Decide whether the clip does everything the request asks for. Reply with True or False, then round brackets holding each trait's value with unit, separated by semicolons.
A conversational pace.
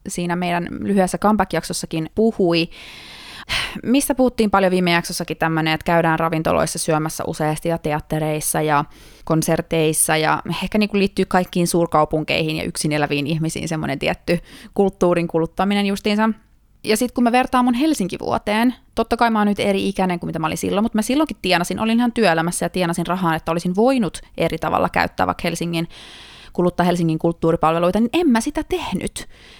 False (165 wpm)